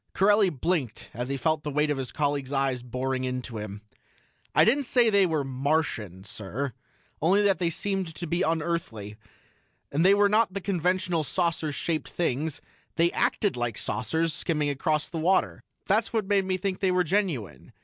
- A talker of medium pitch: Yes, medium, 160 Hz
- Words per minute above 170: Yes, average, 180 wpm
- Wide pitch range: Yes, wide, 5.9 semitones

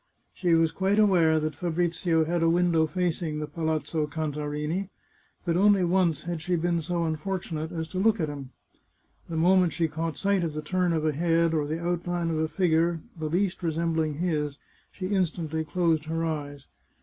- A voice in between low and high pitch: Yes, medium, 165 Hz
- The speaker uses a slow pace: No, average, 190 wpm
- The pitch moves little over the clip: Yes, narrow, 2.1 semitones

